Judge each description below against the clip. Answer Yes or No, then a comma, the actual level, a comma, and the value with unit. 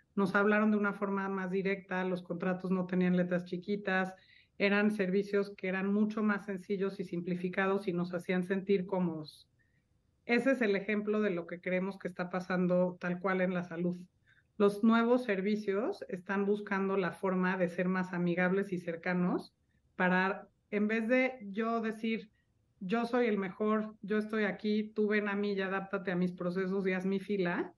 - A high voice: Yes, high, 195 Hz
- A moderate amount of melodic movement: No, narrow, 2.1 semitones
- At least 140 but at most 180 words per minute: Yes, average, 175 wpm